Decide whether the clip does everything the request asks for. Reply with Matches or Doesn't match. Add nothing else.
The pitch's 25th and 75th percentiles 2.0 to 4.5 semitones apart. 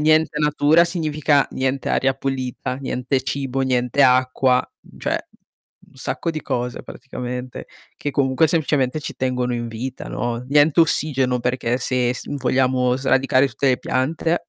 Matches